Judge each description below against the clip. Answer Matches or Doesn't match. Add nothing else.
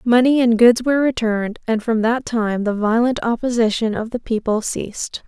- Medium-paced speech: Matches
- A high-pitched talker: Matches